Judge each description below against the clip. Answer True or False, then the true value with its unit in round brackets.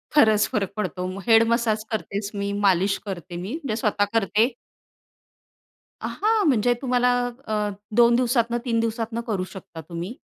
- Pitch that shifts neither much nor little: True (3.0 semitones)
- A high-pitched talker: True (220 Hz)